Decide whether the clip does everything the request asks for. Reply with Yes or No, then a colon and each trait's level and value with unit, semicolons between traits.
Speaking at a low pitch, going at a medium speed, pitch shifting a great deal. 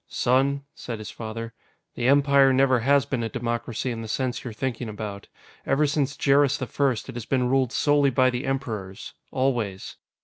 No: low, 130 Hz; average, 180 wpm; average, 3.1 semitones